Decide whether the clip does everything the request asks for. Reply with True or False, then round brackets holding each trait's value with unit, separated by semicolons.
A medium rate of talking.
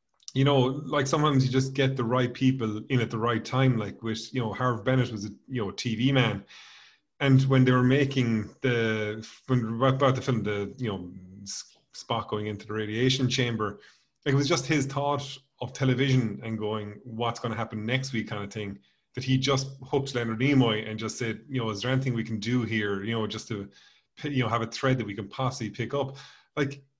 False (220 wpm)